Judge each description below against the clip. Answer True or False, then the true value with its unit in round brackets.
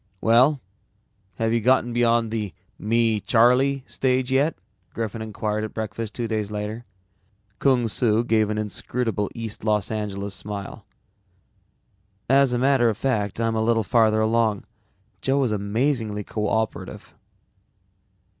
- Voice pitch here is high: False (115 Hz)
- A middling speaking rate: False (130 wpm)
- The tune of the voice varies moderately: False (2.3 semitones)